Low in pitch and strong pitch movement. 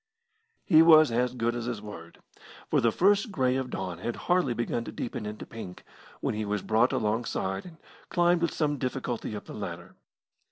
Yes: low, 120 Hz; wide, 6.3 semitones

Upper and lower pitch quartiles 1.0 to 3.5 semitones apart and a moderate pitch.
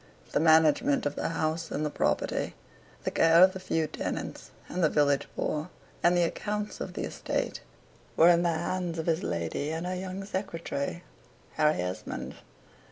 Yes: average, 2.8 semitones; medium, 165 Hz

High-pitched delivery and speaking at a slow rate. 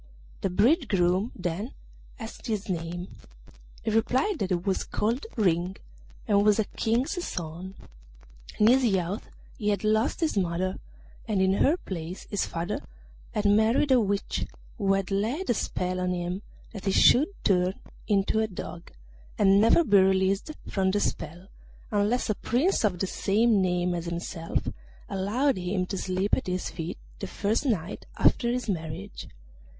No: high, 195 Hz; average, 160 wpm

